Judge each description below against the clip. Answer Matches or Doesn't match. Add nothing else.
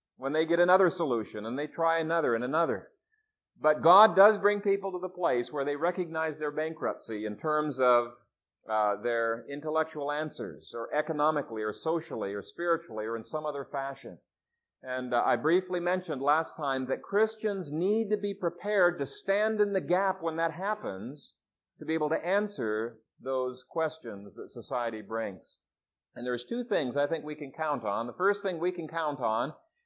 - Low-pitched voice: Doesn't match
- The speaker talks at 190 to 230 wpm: Doesn't match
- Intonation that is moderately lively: Doesn't match